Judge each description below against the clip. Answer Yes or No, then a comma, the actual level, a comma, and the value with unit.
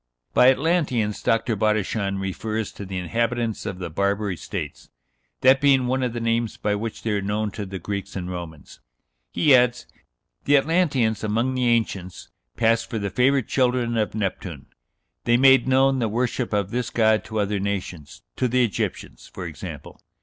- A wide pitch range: No, average, 3.9 semitones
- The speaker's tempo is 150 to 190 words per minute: Yes, average, 170 wpm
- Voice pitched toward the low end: Yes, low, 110 Hz